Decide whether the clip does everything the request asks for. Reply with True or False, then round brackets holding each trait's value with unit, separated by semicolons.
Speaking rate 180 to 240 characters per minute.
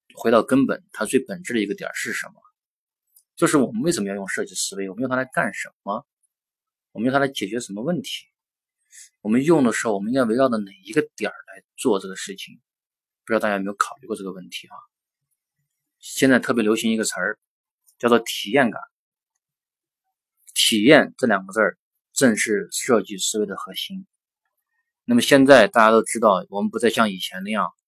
False (290 characters per minute)